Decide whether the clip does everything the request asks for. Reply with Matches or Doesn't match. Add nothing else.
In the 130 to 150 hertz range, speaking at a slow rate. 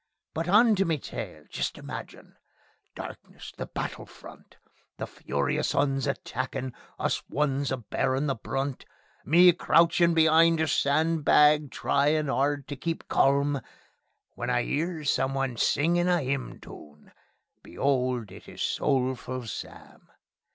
Matches